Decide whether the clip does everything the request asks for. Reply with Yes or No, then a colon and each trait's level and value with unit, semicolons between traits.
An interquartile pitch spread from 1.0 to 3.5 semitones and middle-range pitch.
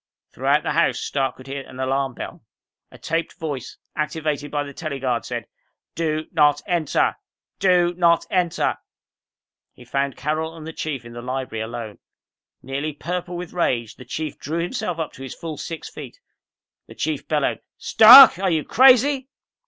No: average, 4.3 semitones; medium, 155 Hz